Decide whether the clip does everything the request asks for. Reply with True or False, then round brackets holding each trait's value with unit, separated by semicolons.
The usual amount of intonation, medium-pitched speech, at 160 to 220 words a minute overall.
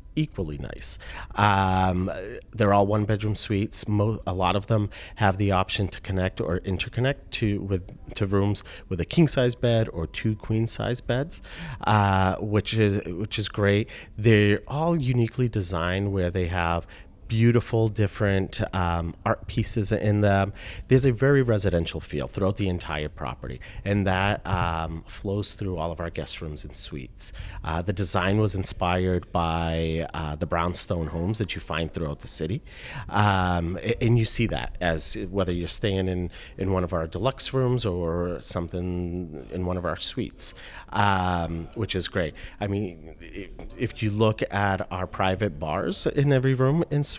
False (3.7 semitones; 95 Hz; 165 wpm)